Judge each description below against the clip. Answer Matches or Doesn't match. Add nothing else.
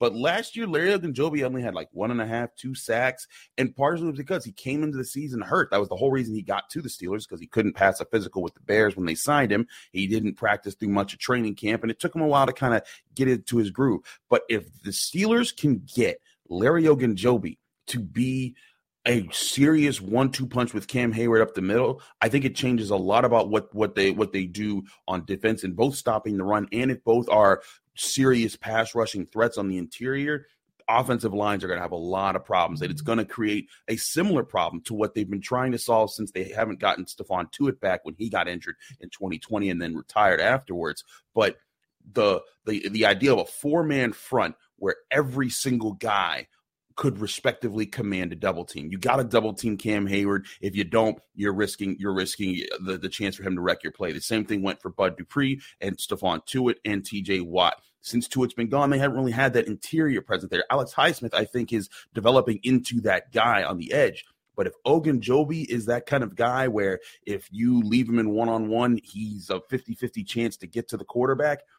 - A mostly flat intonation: Doesn't match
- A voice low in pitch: Matches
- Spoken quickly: Matches